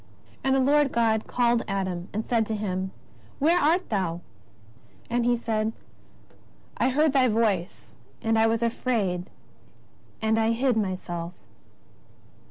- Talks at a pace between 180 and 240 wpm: No, slow, 135 wpm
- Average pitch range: Yes, average, 3.9 semitones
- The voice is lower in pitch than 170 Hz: No, high, 225 Hz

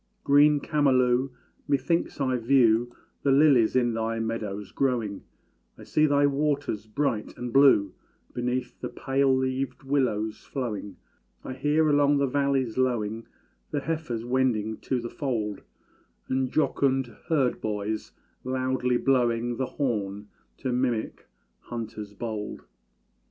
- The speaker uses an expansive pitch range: No, average, 3.5 semitones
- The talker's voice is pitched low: Yes, low, 125 Hz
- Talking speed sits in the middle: No, slow, 125 wpm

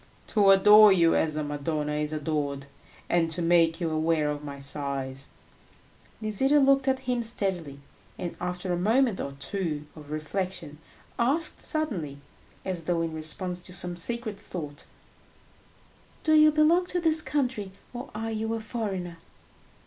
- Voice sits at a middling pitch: Yes, medium, 180 Hz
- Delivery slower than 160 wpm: Yes, average, 150 wpm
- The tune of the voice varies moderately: No, wide, 6.7 semitones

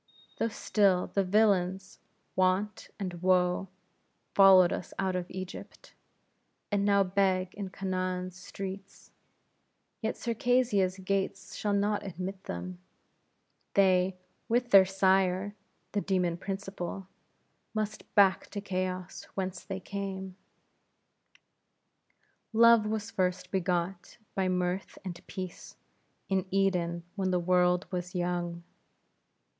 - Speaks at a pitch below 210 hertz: Yes, high, 190 Hz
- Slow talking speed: Yes, slow, 110 wpm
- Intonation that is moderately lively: No, narrow, 1.5 semitones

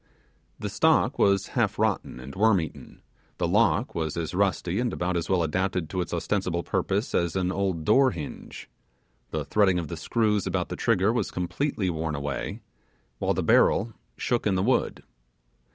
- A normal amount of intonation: Yes, average, 3.6 semitones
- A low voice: Yes, very low, 95 Hz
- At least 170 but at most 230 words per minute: Yes, average, 175 wpm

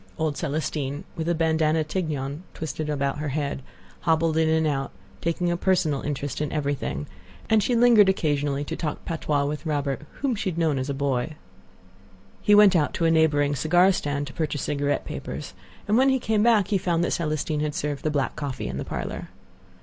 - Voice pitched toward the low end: No, medium, 155 Hz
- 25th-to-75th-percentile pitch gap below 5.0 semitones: Yes, average, 3.1 semitones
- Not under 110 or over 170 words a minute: No, average, 195 wpm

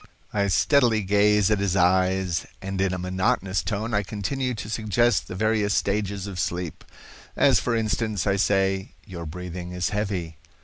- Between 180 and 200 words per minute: No, average, 165 wpm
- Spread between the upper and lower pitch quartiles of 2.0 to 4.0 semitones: Yes, narrow, 2.6 semitones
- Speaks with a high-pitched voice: No, low, 100 Hz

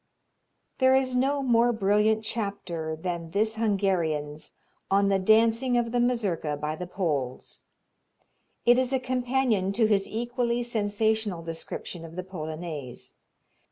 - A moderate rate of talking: No, slow, 130 wpm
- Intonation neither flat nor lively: No, wide, 5.8 semitones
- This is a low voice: No, high, 205 Hz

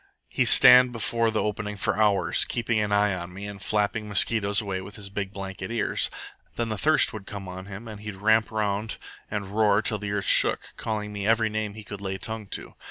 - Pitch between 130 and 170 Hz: No, low, 105 Hz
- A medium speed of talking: No, fast, 220 wpm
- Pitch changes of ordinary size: No, narrow, 1.6 semitones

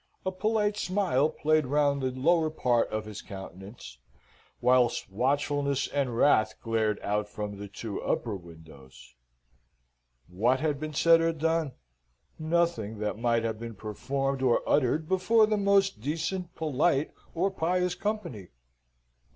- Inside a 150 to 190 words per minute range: No, average, 140 wpm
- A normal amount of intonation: No, wide, 7.2 semitones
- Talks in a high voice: No, medium, 140 Hz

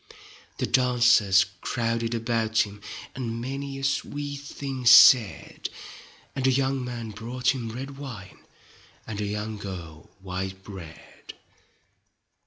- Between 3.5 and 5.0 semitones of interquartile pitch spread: Yes, average, 4.3 semitones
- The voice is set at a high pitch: No, low, 115 Hz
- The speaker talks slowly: Yes, slow, 120 wpm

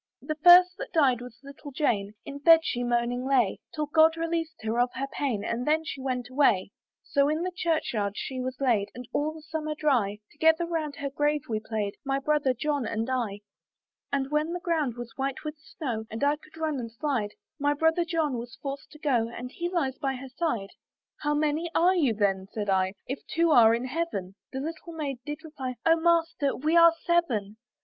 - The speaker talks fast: Yes, fast, 210 wpm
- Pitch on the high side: Yes, very high, 280 Hz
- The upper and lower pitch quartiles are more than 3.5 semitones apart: Yes, average, 4.7 semitones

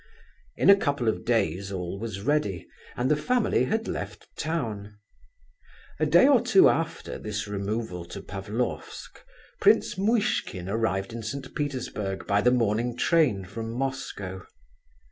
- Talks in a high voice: No, low, 115 Hz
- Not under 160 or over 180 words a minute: No, average, 140 wpm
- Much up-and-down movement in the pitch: Yes, wide, 6.7 semitones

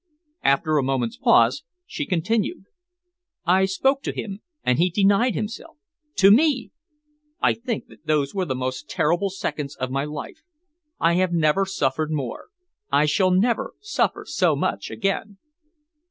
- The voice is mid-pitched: Yes, medium, 180 Hz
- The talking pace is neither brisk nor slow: Yes, average, 150 wpm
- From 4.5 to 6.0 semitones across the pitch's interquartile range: Yes, wide, 5.6 semitones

